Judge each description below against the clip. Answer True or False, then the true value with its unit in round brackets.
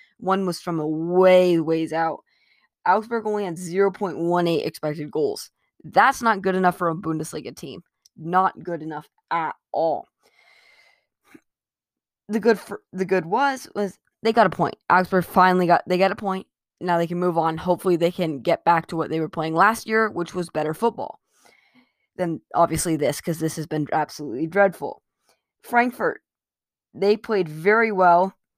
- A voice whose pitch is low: False (180 Hz)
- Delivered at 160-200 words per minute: True (170 wpm)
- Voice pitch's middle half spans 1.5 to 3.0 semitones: False (4.2 semitones)